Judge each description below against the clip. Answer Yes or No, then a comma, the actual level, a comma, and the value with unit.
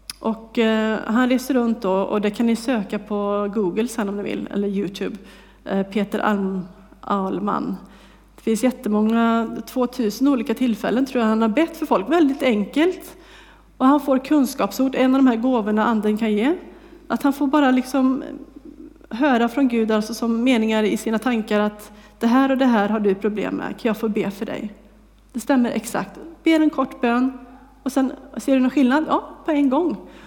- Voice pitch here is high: Yes, high, 235 Hz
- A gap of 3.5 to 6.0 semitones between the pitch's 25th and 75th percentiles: Yes, average, 4.1 semitones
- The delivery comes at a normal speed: Yes, average, 185 wpm